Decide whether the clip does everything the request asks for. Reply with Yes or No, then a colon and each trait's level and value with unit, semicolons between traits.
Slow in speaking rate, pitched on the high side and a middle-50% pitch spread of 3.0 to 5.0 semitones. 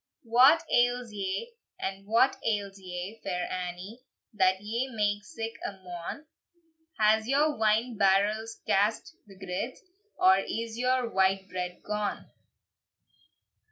Yes: slow, 120 wpm; high, 210 Hz; average, 3.4 semitones